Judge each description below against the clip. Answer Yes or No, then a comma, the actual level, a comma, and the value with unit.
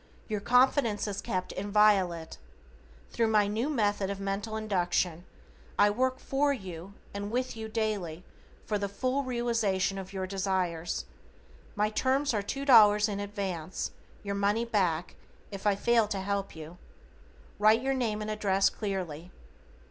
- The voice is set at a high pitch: Yes, high, 205 Hz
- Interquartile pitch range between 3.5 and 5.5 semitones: No, average, 2.7 semitones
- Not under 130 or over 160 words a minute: Yes, average, 145 wpm